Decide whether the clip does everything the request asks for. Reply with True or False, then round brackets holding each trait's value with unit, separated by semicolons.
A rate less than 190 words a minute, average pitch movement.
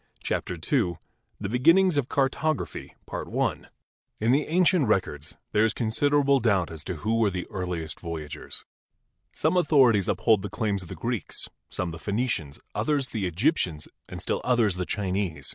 False (155 wpm; 6.9 semitones)